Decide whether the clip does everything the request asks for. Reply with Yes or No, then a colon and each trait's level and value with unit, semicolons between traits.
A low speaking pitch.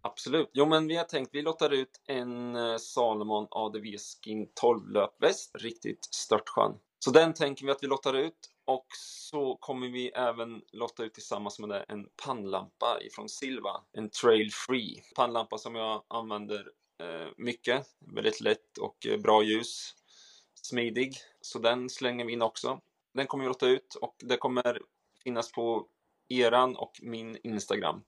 Yes: low, 120 Hz